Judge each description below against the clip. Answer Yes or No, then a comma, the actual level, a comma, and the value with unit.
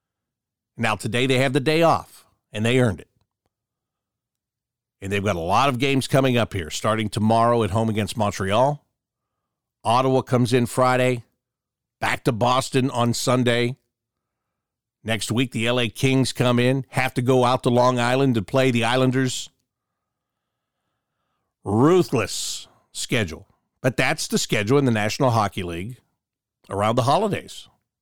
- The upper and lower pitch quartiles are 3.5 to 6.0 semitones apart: No, narrow, 2.6 semitones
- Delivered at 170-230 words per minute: No, average, 145 wpm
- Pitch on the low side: Yes, low, 125 Hz